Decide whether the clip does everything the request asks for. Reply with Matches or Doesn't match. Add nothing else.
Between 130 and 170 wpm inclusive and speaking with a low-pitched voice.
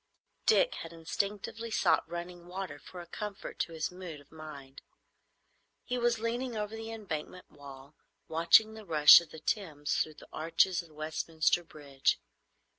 Doesn't match